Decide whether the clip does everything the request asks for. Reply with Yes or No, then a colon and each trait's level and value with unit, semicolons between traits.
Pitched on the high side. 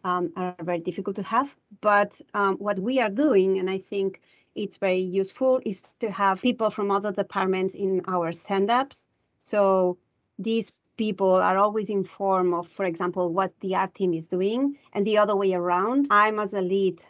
Yes: high, 195 Hz